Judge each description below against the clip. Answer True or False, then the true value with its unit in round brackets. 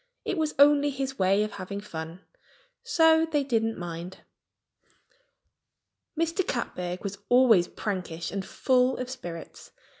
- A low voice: False (225 Hz)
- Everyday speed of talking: False (125 wpm)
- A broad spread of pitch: True (7.2 semitones)